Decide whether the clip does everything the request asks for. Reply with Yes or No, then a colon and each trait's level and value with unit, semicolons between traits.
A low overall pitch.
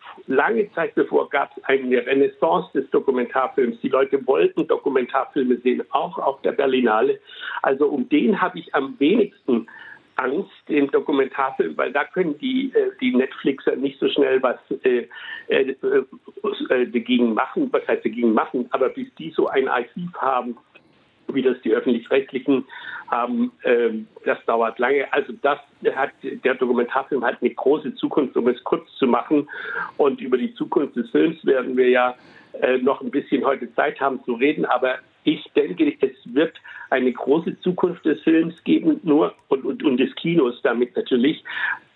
No: very high, 270 Hz